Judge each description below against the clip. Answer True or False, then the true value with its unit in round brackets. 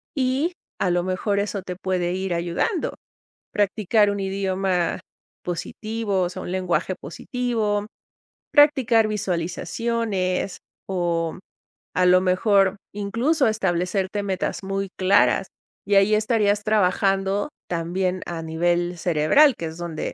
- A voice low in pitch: False (195 Hz)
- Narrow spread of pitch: False (3.0 semitones)